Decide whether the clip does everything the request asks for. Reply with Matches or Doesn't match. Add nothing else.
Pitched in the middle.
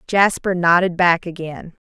Matches